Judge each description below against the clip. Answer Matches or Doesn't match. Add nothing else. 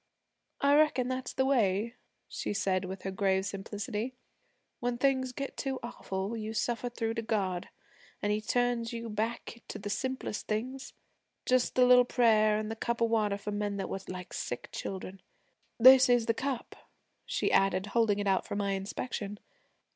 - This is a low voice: Doesn't match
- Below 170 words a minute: Doesn't match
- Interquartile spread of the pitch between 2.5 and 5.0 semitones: Matches